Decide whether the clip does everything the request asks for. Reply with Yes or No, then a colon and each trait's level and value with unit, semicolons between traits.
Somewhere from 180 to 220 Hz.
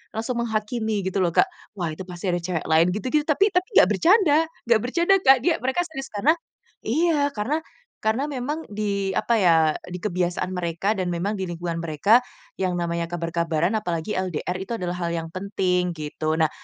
Yes: high, 190 Hz